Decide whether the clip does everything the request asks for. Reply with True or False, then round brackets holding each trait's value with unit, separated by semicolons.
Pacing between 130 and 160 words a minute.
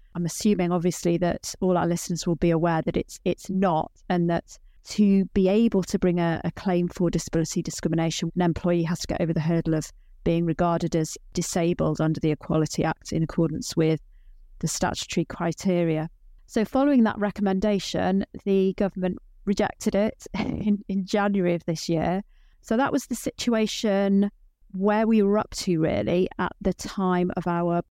False (170 wpm)